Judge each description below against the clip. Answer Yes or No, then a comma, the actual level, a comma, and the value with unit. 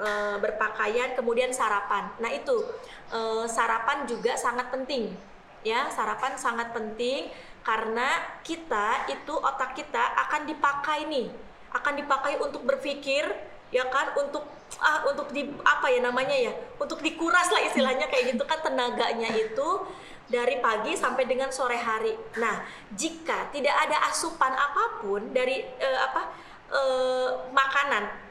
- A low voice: No, very high, 280 Hz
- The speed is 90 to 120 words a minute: No, average, 130 wpm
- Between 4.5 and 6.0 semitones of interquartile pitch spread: Yes, average, 5.1 semitones